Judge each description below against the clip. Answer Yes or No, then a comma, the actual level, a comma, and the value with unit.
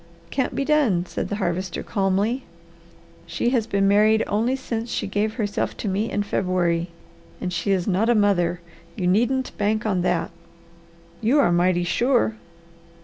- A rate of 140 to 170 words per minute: Yes, average, 160 wpm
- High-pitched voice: Yes, high, 205 Hz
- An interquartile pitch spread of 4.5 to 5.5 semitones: No, average, 3.9 semitones